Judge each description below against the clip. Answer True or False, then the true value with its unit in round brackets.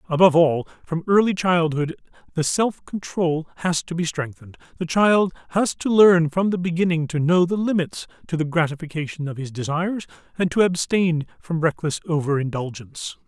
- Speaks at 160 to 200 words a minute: True (165 wpm)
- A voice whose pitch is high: False (165 Hz)